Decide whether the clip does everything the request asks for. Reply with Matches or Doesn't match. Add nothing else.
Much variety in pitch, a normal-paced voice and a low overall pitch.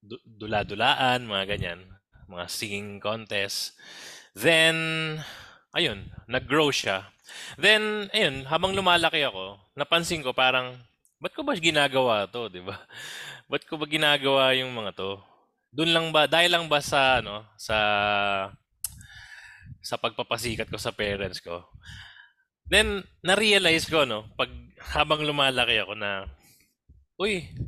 Matches